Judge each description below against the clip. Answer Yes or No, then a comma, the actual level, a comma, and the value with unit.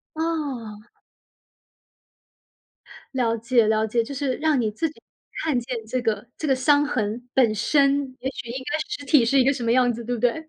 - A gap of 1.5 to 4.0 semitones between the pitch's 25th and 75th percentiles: Yes, average, 3.7 semitones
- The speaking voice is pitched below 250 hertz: No, very high, 255 Hz